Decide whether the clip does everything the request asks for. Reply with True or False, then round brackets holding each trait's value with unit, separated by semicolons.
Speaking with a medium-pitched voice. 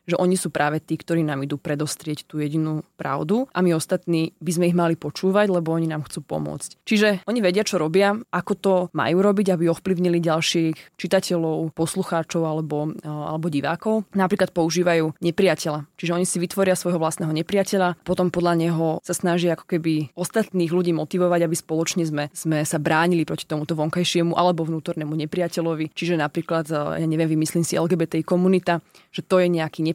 True (170 Hz)